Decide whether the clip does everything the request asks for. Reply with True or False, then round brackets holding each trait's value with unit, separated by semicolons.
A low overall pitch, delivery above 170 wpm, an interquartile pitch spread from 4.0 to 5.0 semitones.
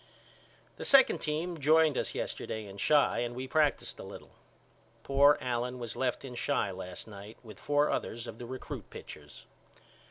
False (125 Hz; 165 wpm; 4.7 semitones)